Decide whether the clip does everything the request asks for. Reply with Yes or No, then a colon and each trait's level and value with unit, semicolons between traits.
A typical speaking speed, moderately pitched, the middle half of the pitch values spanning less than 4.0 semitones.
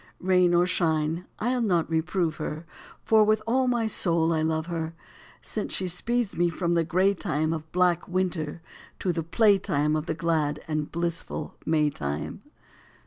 Yes: average, 175 wpm; medium, 170 Hz; average, 2.8 semitones